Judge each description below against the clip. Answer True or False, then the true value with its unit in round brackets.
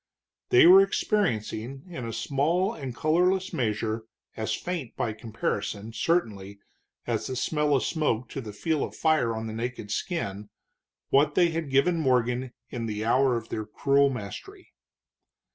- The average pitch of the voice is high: False (130 Hz)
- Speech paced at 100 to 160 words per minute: True (155 wpm)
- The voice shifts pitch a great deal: True (6.5 semitones)